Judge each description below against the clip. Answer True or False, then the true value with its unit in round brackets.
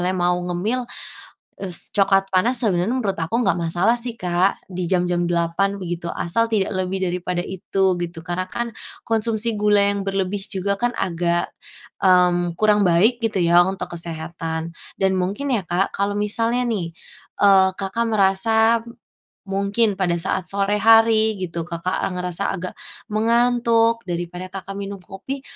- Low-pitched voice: False (195 Hz)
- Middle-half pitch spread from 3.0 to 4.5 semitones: True (3.5 semitones)